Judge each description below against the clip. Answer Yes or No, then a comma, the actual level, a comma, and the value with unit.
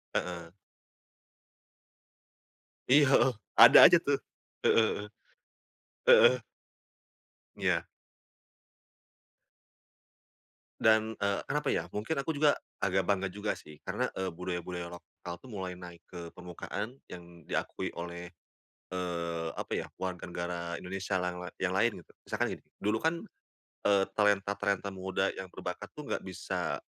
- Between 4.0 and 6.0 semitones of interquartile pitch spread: No, average, 2.9 semitones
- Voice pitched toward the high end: No, very low, 95 Hz